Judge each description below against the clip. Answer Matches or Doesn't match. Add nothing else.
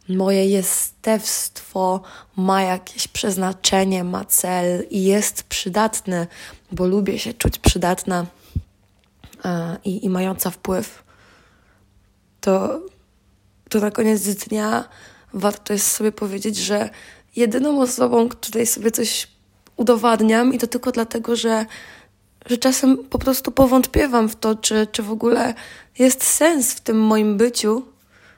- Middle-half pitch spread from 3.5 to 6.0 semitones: Matches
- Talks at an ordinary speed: Matches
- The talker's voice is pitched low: Doesn't match